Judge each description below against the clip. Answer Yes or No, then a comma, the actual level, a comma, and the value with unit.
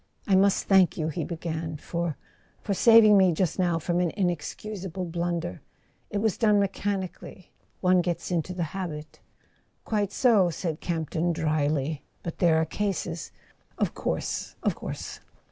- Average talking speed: Yes, average, 145 wpm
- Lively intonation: No, average, 3.2 semitones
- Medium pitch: Yes, medium, 175 Hz